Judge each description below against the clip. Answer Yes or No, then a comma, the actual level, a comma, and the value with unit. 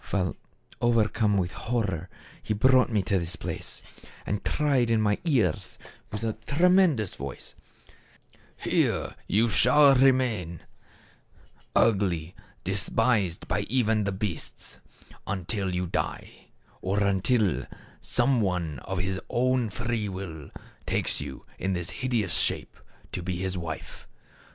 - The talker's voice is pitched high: No, low, 105 Hz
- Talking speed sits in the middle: No, slow, 125 wpm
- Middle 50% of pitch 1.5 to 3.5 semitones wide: No, average, 4.6 semitones